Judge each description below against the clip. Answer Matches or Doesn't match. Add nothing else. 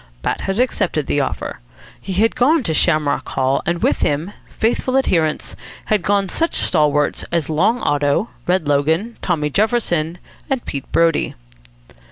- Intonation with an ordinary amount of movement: Doesn't match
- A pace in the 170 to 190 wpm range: Doesn't match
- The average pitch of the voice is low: Doesn't match